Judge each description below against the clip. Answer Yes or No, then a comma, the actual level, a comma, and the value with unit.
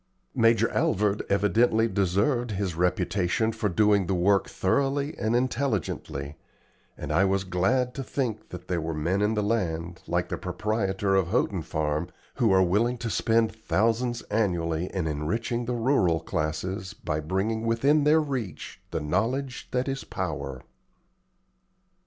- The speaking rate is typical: Yes, average, 145 wpm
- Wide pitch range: No, average, 4.5 semitones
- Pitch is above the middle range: No, low, 100 Hz